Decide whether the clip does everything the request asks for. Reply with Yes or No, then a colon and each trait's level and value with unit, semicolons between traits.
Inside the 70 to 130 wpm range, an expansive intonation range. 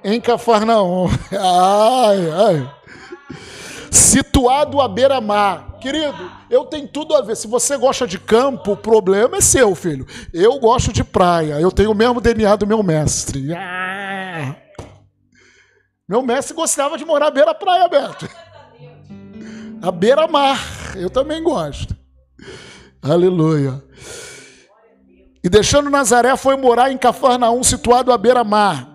Yes: slow, 120 wpm; wide, 7.1 semitones